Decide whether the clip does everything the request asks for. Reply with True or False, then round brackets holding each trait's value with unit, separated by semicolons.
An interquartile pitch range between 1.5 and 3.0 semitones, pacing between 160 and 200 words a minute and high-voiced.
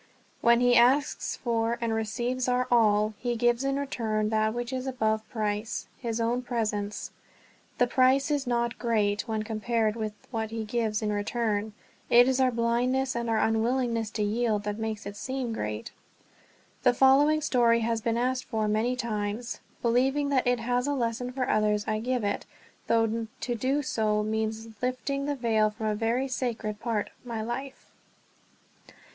True (2.4 semitones; 170 wpm; 235 Hz)